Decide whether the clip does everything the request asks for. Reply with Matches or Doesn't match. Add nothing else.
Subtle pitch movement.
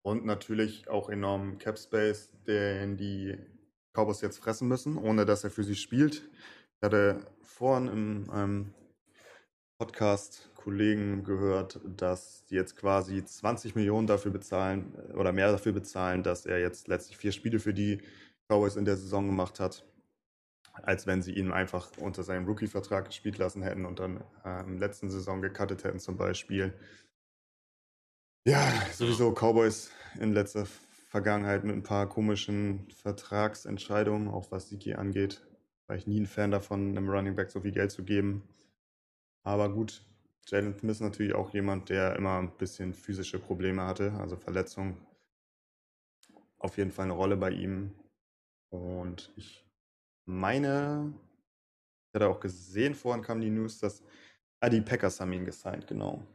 Matches